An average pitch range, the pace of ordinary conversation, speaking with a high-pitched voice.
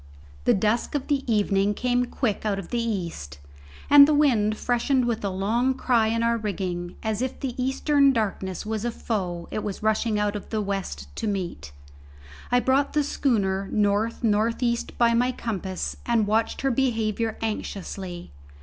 Yes: average, 3.6 semitones; average, 175 wpm; high, 220 Hz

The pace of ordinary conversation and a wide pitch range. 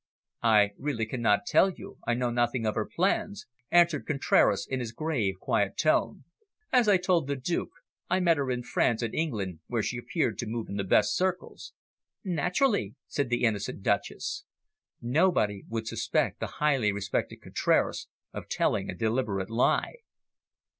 Yes: average, 160 wpm; wide, 7.0 semitones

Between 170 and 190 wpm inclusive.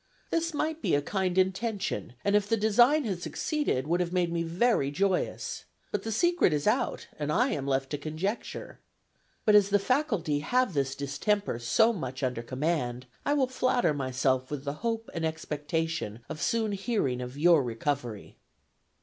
Yes: average, 175 wpm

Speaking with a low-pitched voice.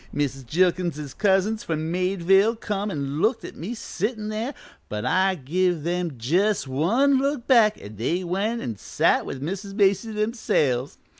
No: medium, 185 Hz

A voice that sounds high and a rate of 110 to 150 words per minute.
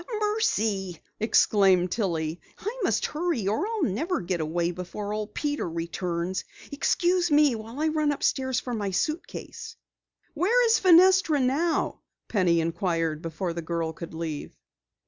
Yes: high, 215 Hz; average, 140 wpm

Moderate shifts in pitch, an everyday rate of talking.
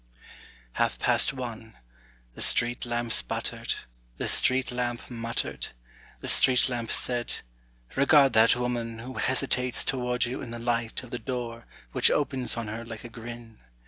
No: narrow, 1.5 semitones; average, 150 wpm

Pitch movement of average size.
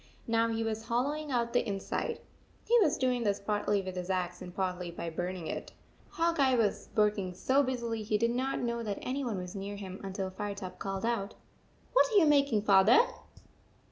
Yes: average, 4.4 semitones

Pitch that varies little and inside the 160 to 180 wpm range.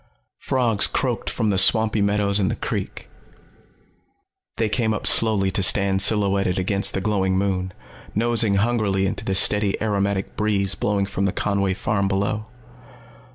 No: narrow, 1.8 semitones; average, 150 wpm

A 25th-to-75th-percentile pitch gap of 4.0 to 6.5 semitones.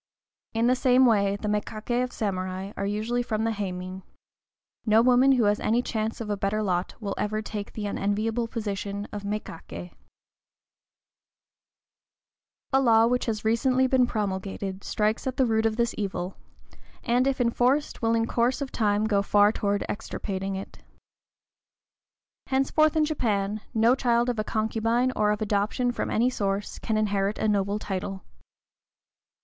No: average, 3.0 semitones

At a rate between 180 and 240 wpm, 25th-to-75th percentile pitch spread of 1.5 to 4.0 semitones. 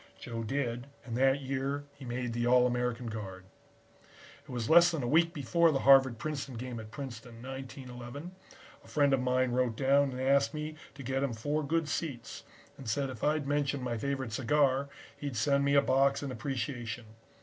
Yes: average, 190 wpm; average, 2.7 semitones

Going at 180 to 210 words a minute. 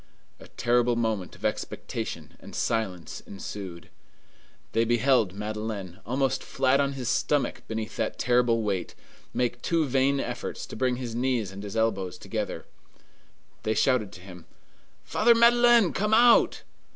No: average, 140 wpm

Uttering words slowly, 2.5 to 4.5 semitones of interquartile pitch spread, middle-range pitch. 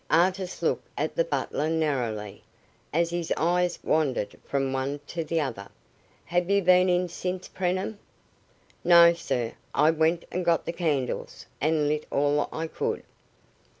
No: average, 150 wpm; average, 3.5 semitones; medium, 165 Hz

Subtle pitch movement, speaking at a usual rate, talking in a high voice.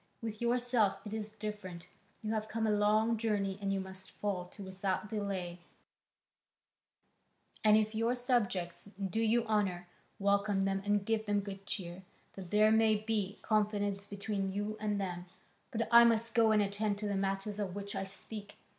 Yes: narrow, 1.9 semitones; average, 170 wpm; high, 205 Hz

